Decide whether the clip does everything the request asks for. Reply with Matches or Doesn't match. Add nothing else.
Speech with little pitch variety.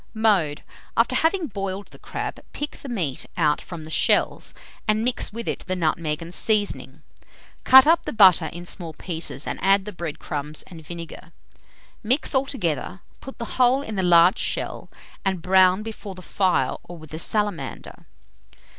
Doesn't match